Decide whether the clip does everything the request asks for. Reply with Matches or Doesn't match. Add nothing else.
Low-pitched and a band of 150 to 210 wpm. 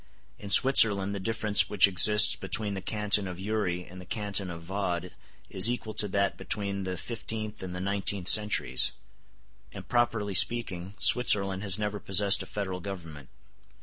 Matches